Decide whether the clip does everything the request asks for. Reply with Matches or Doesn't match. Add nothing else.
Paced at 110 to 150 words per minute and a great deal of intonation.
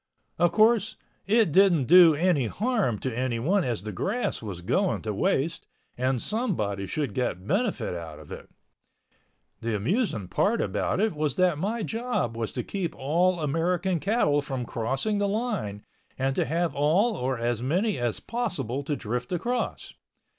Doesn't match